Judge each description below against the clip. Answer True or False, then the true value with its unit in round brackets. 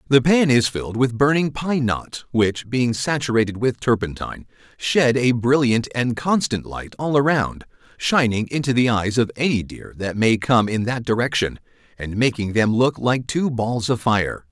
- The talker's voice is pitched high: False (120 Hz)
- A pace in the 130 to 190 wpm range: True (180 wpm)